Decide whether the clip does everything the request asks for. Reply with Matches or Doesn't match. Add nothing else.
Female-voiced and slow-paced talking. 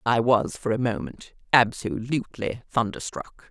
Matches